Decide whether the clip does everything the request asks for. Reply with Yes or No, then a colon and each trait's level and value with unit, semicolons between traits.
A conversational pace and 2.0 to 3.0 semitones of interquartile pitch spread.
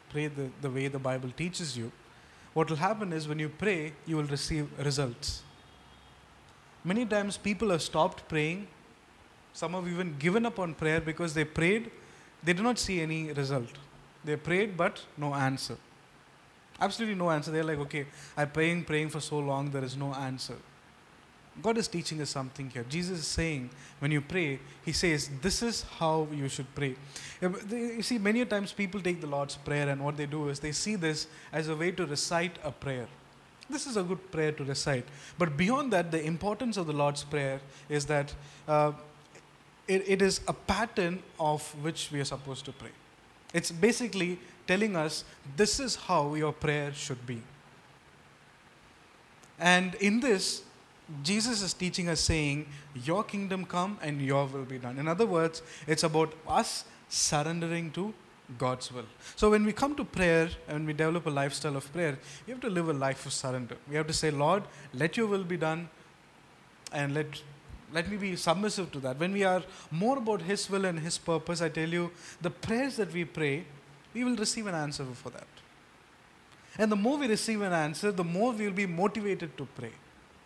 No: average, 190 wpm; average, 4.4 semitones